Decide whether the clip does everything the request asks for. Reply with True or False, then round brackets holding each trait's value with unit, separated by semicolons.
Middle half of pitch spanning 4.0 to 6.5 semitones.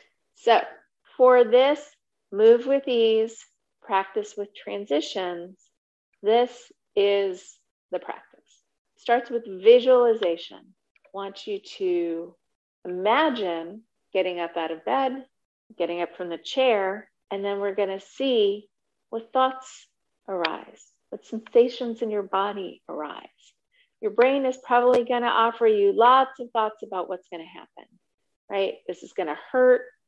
True (4.6 semitones)